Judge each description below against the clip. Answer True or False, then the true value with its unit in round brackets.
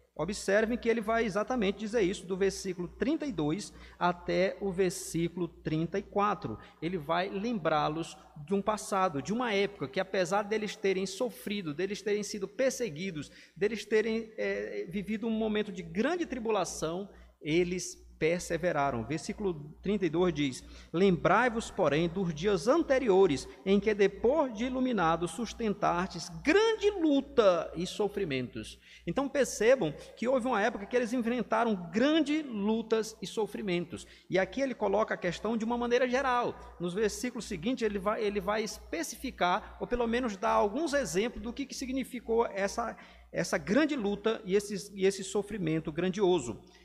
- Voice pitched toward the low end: False (205 Hz)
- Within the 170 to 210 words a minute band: False (145 wpm)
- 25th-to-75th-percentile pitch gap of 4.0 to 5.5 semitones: True (4.3 semitones)